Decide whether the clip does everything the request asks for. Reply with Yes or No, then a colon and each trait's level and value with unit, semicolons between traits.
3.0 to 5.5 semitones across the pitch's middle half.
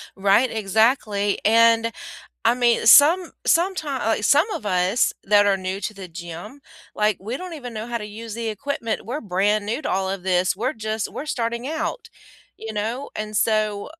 Yes: average, 3.3 semitones